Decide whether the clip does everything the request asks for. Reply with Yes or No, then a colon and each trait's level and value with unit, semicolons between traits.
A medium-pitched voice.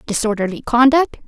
No: high, 240 Hz